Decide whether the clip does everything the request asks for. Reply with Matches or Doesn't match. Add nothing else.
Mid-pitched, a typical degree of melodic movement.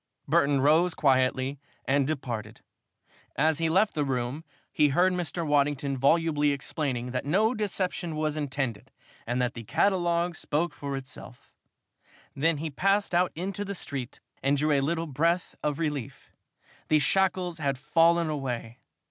Matches